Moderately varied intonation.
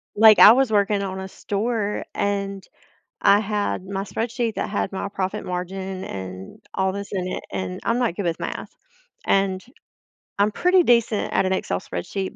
No: narrow, 2.1 semitones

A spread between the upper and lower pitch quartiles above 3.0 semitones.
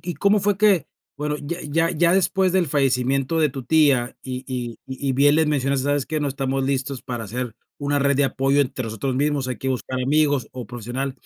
No: narrow, 2.6 semitones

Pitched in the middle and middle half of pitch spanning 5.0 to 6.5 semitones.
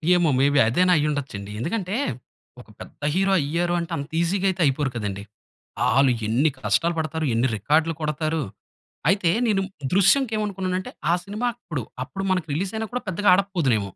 Yes: medium, 165 Hz; wide, 5.4 semitones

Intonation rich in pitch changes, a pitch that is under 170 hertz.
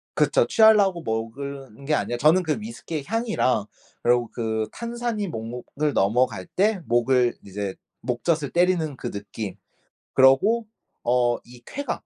Yes: wide, 7.7 semitones; low, 135 Hz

